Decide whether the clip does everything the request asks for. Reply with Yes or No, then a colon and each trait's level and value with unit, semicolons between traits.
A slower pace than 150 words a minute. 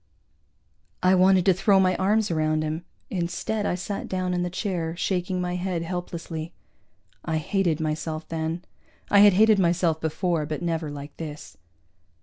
No: average, 155 wpm